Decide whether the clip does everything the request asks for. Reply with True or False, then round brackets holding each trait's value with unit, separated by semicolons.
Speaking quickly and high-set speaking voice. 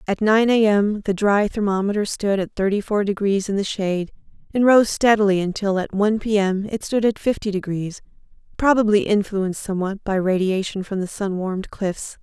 False (185 wpm; 200 Hz)